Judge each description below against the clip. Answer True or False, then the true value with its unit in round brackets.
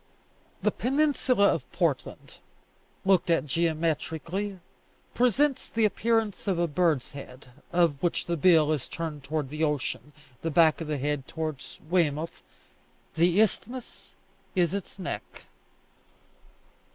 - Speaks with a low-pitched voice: False (165 Hz)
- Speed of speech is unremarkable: False (125 wpm)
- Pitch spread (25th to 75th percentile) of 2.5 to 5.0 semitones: True (4.3 semitones)